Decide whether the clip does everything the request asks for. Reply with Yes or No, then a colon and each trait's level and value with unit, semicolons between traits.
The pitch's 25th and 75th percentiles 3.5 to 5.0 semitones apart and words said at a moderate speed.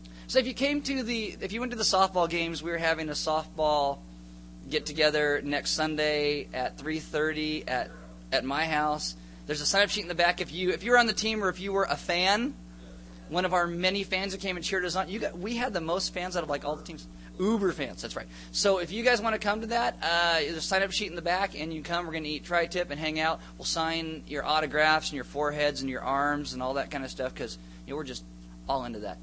No: average, 4.6 semitones; fast, 270 wpm